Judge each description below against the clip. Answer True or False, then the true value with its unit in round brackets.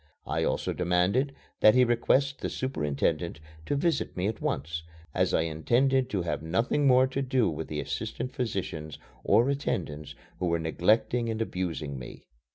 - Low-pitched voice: True (100 Hz)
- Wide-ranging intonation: True (8.0 semitones)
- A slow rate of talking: False (165 wpm)